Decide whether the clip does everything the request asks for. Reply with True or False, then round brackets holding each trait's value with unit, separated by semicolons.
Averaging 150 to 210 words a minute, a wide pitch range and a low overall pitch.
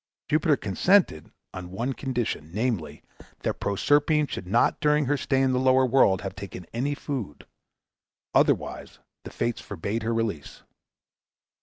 False (140 wpm; 5.9 semitones; 120 Hz)